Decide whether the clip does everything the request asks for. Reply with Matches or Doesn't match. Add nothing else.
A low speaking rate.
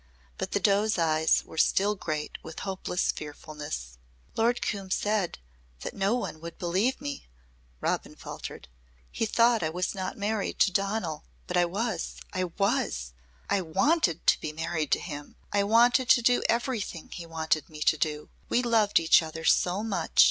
Doesn't match